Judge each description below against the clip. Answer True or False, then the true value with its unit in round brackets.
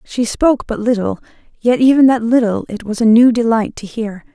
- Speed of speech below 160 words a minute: False (205 wpm)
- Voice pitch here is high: True (230 Hz)